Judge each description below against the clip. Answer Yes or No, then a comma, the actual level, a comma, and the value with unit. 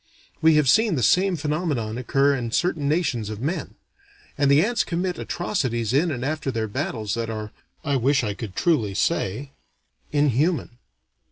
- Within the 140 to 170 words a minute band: Yes, average, 165 wpm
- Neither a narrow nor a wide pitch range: No, wide, 5.7 semitones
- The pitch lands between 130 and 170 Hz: Yes, medium, 140 Hz